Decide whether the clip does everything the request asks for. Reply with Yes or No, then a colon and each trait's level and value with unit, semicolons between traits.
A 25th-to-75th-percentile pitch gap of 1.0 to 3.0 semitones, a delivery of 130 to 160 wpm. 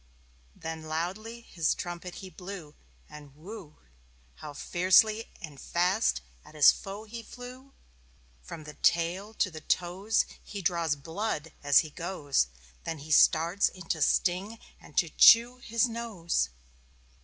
No: average, 5.3 semitones; average, 140 wpm